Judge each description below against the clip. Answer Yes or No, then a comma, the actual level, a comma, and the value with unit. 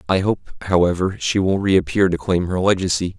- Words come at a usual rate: Yes, average, 190 wpm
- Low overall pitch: Yes, very low, 95 Hz